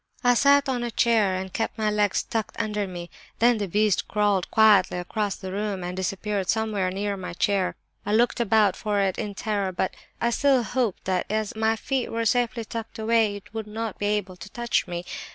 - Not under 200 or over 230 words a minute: Yes, fast, 205 wpm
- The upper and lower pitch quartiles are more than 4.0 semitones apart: No, average, 2.7 semitones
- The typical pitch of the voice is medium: No, high, 210 Hz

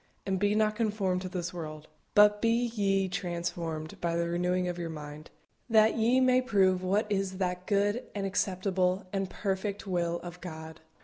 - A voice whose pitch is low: No, medium, 185 Hz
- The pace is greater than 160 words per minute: Yes, average, 175 wpm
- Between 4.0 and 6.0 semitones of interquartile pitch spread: No, average, 3.0 semitones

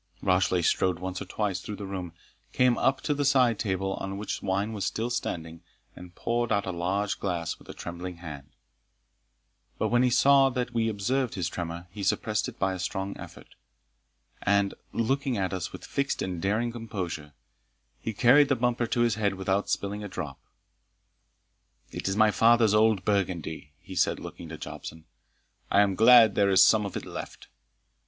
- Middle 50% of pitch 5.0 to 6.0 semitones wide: No, average, 4.1 semitones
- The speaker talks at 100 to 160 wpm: No, average, 180 wpm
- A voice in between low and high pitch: No, low, 100 Hz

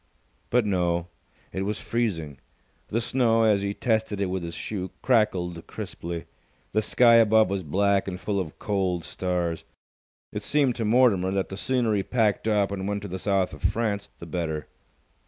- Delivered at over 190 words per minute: No, average, 175 wpm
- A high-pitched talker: No, low, 100 Hz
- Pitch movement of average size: Yes, average, 3.4 semitones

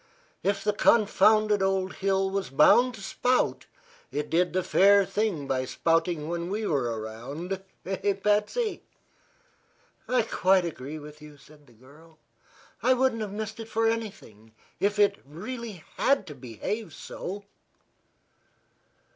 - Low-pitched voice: No, high, 190 Hz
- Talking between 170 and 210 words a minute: No, average, 140 wpm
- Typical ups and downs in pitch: No, wide, 5.9 semitones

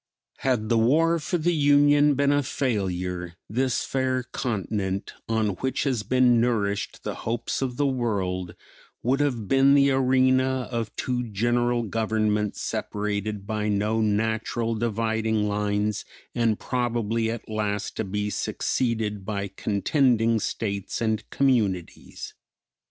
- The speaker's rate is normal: No, slow, 130 wpm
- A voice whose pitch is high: No, low, 115 Hz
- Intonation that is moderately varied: Yes, average, 3.7 semitones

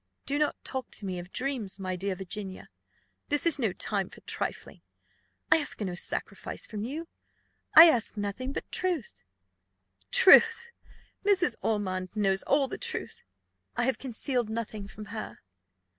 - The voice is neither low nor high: No, high, 220 Hz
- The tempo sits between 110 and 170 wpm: Yes, average, 150 wpm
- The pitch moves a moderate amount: No, wide, 6.1 semitones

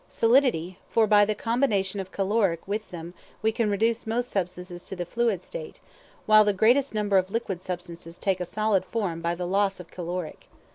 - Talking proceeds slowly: No, average, 190 wpm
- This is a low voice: No, high, 200 Hz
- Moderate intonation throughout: Yes, average, 3.6 semitones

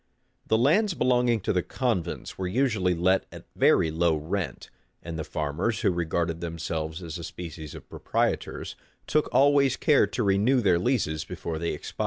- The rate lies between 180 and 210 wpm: No, average, 170 wpm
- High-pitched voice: No, very low, 90 Hz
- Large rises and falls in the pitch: Yes, wide, 6.7 semitones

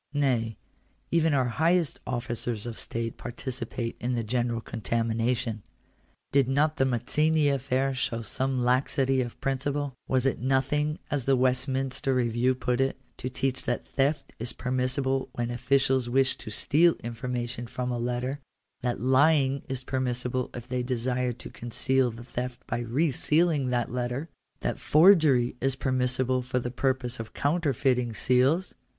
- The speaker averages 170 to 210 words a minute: No, average, 155 wpm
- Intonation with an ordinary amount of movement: No, narrow, 1.9 semitones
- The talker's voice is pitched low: Yes, low, 130 Hz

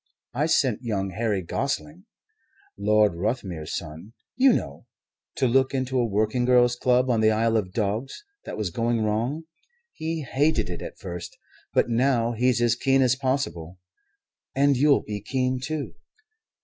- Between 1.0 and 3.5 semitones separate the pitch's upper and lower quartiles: No, average, 3.9 semitones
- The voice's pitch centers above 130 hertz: No, low, 120 Hz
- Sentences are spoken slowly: No, average, 155 wpm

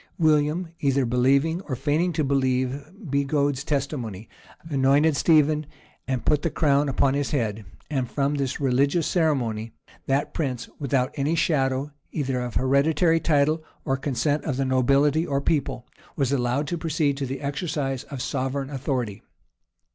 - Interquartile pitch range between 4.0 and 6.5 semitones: No, narrow, 2.4 semitones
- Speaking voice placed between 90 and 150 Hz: Yes, medium, 140 Hz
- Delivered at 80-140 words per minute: No, average, 150 wpm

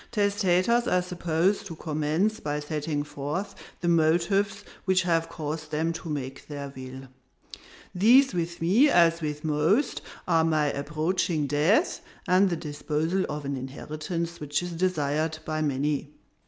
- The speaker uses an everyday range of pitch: Yes, average, 3.6 semitones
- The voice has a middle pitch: Yes, medium, 165 Hz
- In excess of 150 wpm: No, average, 140 wpm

